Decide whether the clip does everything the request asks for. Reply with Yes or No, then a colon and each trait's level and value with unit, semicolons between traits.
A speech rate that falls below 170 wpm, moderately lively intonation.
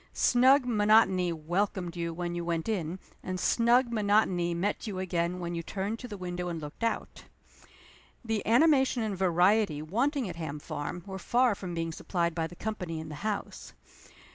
No: average, 175 wpm; average, 4.3 semitones